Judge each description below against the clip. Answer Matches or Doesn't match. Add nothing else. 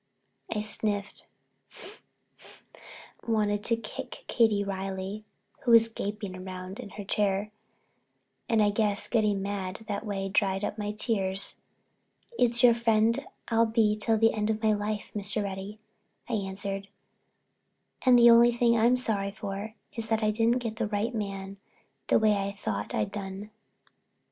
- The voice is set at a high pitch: Matches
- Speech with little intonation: Matches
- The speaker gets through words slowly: Doesn't match